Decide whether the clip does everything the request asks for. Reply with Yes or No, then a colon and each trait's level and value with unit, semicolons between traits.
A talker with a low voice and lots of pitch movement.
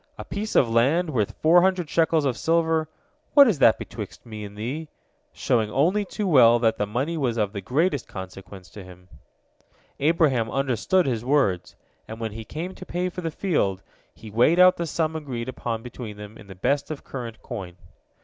Yes: low, 130 Hz; wide, 6.9 semitones